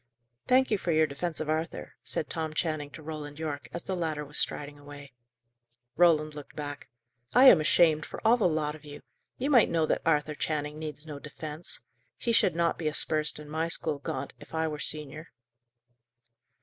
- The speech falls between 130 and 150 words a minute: No, average, 190 wpm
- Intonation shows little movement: Yes, narrow, 1.8 semitones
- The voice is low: No, medium, 155 Hz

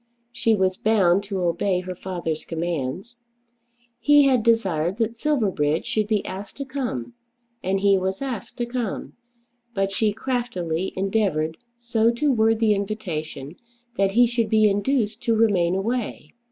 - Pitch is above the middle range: Yes, high, 205 Hz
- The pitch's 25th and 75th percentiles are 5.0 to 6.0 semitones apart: No, average, 4.1 semitones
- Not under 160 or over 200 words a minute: No, average, 150 wpm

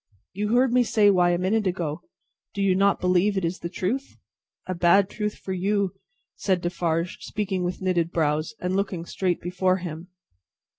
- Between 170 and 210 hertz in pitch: Yes, medium, 185 Hz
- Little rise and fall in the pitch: Yes, narrow, 2.3 semitones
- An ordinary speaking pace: Yes, average, 180 wpm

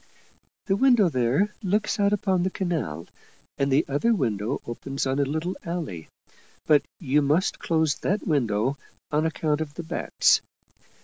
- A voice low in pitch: No, medium, 155 Hz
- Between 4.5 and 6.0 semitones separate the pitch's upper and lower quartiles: Yes, wide, 5.4 semitones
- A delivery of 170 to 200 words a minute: No, average, 160 wpm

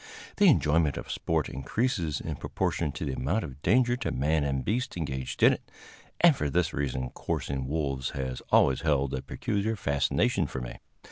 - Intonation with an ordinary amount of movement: No, wide, 6.6 semitones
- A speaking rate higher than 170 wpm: Yes, average, 180 wpm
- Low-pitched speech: Yes, very low, 75 Hz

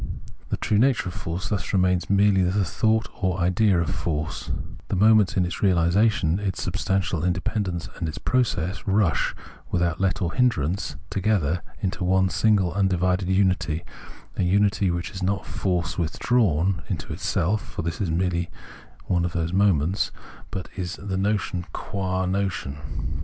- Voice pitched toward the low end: Yes, very low, 95 Hz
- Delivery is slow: No, average, 155 wpm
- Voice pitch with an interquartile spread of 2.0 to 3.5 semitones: Yes, narrow, 2.5 semitones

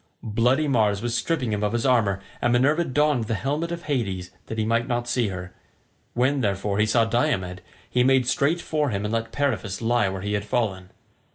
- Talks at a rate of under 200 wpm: No, fast, 205 wpm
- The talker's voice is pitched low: Yes, low, 120 Hz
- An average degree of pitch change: Yes, average, 4.3 semitones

